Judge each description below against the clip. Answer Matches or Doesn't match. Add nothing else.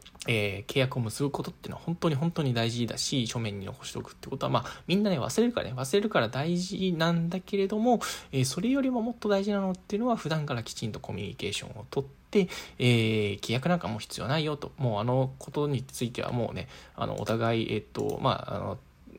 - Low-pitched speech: Doesn't match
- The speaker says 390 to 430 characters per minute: Doesn't match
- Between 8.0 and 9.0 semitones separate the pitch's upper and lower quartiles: Matches